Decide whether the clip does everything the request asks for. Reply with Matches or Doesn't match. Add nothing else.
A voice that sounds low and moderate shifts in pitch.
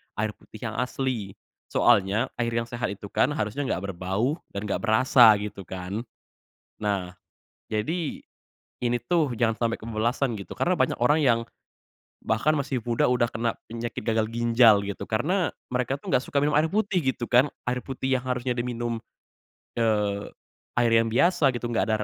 Matches